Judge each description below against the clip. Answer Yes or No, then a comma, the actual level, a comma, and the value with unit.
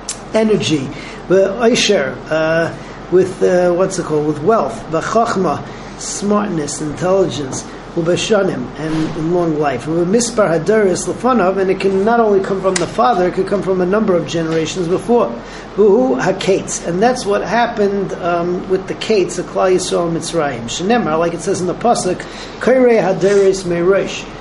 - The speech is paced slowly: No, average, 155 wpm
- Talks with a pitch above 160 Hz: Yes, medium, 185 Hz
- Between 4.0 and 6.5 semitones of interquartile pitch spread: No, average, 3.6 semitones